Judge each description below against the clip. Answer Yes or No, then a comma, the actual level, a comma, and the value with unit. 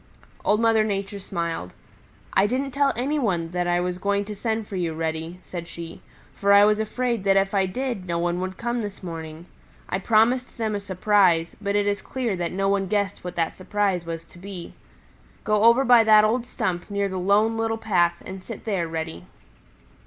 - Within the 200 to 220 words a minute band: Yes, fast, 205 wpm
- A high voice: Yes, high, 200 Hz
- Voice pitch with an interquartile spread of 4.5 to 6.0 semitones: No, average, 3.8 semitones